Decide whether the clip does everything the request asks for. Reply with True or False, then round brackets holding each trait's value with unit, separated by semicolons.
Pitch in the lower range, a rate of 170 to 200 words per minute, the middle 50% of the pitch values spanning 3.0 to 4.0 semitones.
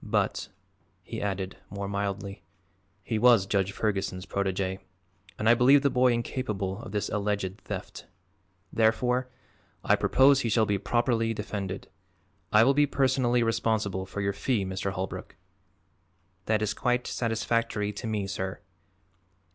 False (105 Hz; 140 wpm; 3.3 semitones)